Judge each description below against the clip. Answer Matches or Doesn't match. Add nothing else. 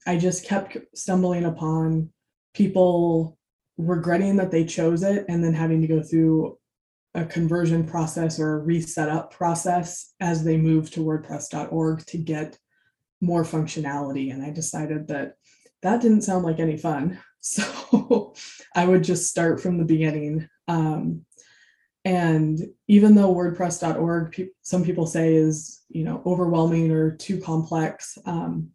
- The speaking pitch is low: Doesn't match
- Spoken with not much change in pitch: Matches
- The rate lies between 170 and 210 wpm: Doesn't match